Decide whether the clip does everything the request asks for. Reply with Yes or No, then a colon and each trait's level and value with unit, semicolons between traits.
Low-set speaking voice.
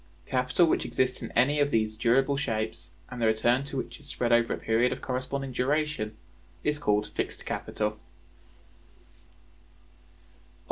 Yes: low, 125 Hz